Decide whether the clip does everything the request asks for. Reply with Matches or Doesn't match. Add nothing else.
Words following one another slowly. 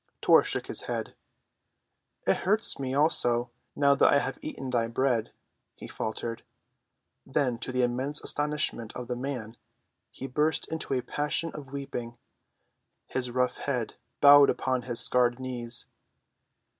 Doesn't match